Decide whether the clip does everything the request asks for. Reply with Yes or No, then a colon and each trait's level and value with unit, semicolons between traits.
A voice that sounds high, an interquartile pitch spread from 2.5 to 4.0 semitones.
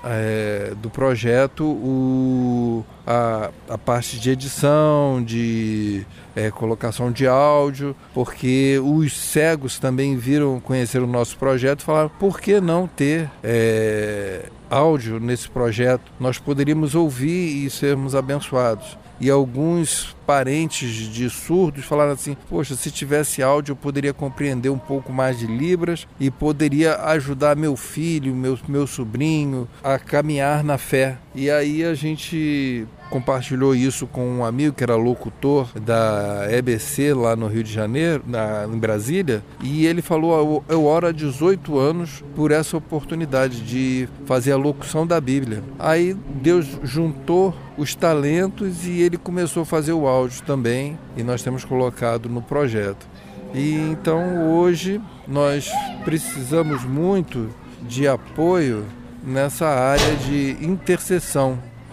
No: medium, 140 Hz; average, 3.7 semitones